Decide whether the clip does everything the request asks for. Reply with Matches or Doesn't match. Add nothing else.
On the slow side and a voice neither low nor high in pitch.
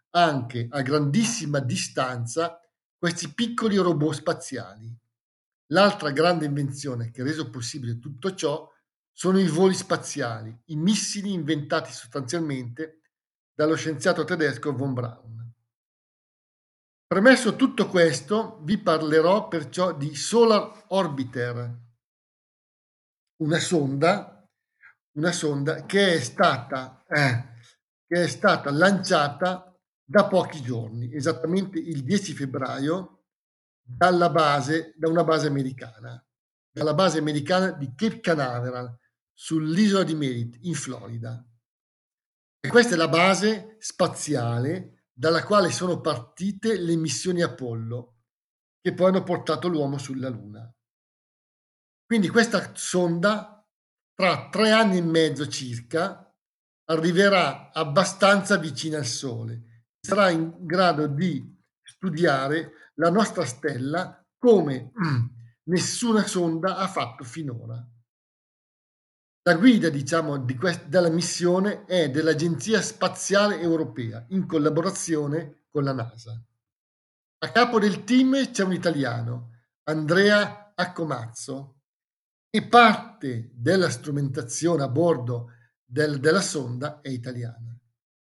Matches